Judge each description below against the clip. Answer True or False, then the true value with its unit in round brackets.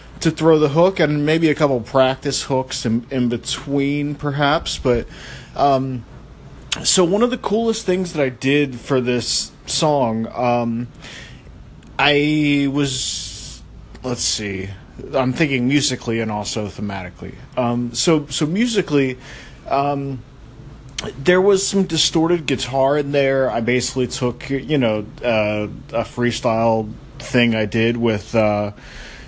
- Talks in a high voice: False (130 Hz)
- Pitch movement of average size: True (3.6 semitones)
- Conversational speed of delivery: False (130 wpm)